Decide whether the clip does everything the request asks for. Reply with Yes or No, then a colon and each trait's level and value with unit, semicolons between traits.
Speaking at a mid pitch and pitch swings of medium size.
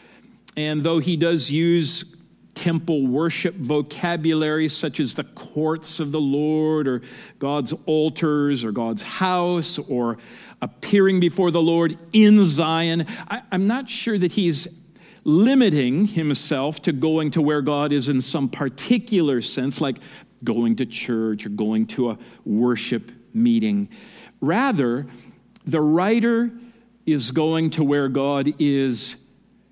Yes: medium, 155 Hz; average, 4.5 semitones